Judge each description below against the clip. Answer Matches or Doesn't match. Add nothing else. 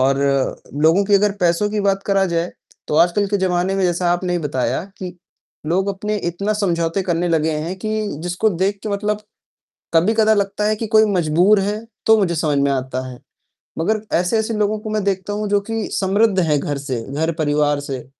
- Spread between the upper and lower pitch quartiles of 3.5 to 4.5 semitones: Matches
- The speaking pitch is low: Doesn't match